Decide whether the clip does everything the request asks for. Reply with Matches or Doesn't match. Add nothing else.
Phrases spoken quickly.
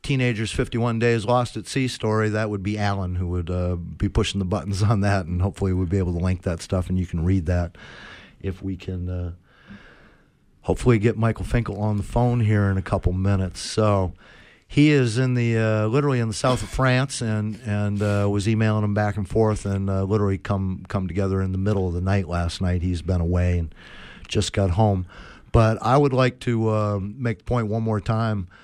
Matches